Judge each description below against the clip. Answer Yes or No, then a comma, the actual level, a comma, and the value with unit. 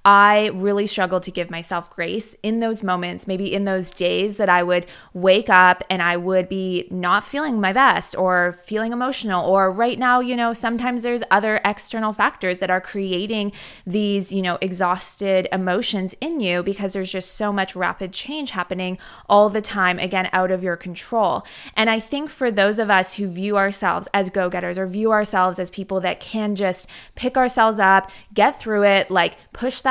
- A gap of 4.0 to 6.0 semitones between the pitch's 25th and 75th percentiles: No, average, 2.7 semitones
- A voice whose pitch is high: Yes, high, 195 Hz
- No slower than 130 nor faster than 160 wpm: No, average, 195 wpm